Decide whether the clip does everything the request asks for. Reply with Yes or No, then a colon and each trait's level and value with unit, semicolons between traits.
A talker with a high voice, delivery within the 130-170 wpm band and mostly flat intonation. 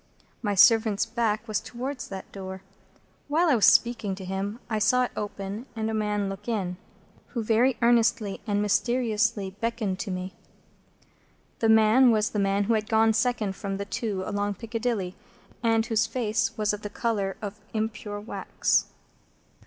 Yes: high, 215 Hz; average, 165 wpm; narrow, 2.3 semitones